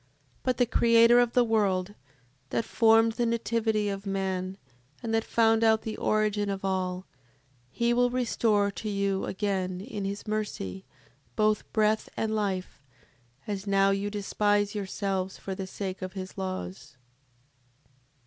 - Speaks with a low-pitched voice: No, high, 205 Hz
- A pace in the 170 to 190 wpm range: No, average, 150 wpm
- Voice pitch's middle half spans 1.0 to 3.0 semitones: Yes, narrow, 2.6 semitones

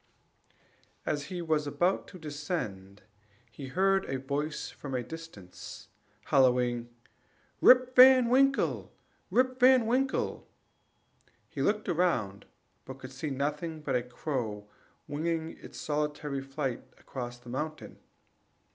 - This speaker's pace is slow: Yes, slow, 120 wpm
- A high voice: No, medium, 150 Hz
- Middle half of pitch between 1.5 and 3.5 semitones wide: No, wide, 5.6 semitones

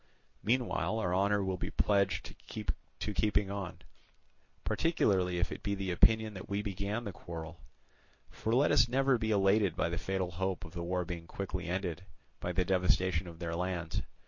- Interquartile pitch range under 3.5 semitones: Yes, average, 2.7 semitones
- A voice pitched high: No, very low, 95 Hz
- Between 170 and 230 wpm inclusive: Yes, average, 175 wpm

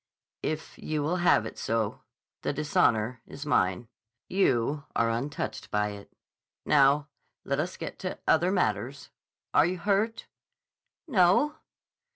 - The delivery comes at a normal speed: No, slow, 130 wpm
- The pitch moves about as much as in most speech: No, wide, 7.5 semitones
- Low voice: No, medium, 145 Hz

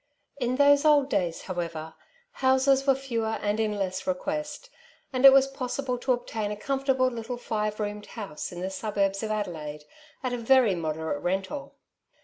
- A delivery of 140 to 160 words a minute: No, average, 170 wpm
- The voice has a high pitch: Yes, high, 225 Hz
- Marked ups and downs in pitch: Yes, wide, 5.7 semitones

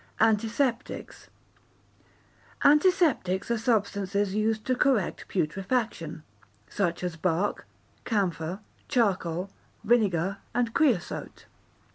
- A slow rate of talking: Yes, slow, 80 wpm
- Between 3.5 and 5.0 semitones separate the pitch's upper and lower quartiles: Yes, average, 4.3 semitones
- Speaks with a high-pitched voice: Yes, high, 205 Hz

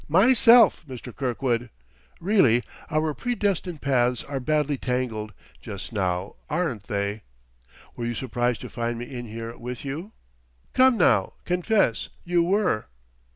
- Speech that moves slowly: Yes, slow, 130 wpm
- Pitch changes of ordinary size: No, wide, 7.0 semitones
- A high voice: No, low, 130 Hz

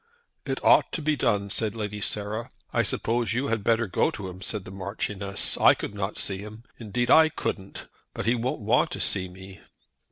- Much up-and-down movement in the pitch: No, average, 3.1 semitones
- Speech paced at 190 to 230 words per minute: Yes, average, 200 wpm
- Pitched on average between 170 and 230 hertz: No, low, 105 Hz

